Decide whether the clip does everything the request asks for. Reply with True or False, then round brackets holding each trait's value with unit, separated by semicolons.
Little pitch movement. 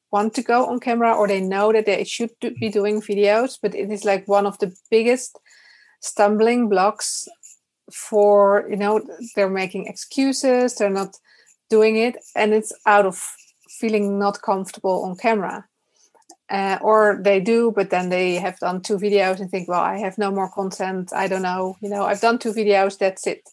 True (2.3 semitones)